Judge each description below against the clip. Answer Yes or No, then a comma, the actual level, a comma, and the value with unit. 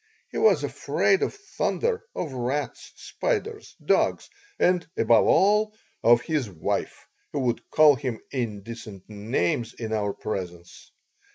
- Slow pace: Yes, slow, 125 wpm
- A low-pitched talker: Yes, low, 125 Hz